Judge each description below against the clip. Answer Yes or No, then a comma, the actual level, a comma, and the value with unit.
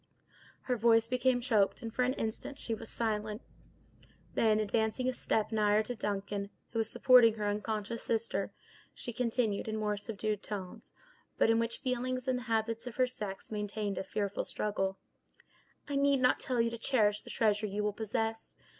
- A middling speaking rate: Yes, average, 180 wpm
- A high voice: Yes, high, 220 Hz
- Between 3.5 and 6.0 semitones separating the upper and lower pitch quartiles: No, narrow, 2.5 semitones